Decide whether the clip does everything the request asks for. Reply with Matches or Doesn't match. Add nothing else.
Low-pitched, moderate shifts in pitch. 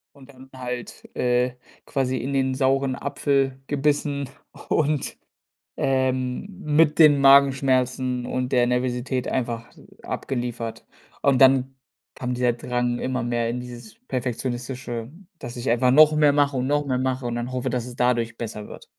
Doesn't match